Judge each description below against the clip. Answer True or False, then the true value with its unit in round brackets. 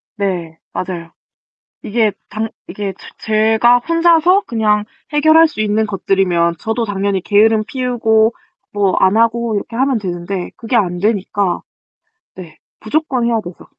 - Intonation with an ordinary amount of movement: True (3.5 semitones)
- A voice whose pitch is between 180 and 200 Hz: False (215 Hz)